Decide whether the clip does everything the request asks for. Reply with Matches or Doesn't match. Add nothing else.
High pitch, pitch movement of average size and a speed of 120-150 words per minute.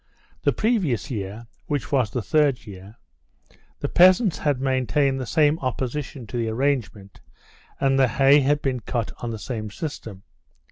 Doesn't match